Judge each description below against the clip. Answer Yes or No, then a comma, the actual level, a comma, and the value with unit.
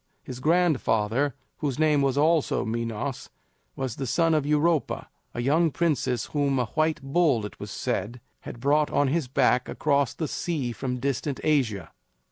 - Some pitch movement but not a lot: Yes, average, 3.8 semitones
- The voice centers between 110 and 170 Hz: Yes, medium, 140 Hz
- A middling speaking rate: Yes, average, 160 wpm